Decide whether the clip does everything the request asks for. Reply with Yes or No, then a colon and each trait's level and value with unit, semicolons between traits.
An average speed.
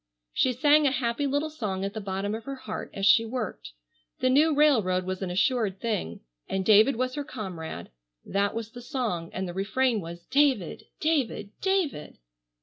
Yes: average, 180 wpm